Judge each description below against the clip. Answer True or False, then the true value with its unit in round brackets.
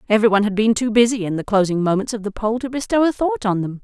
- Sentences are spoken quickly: True (295 wpm)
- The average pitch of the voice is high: True (220 Hz)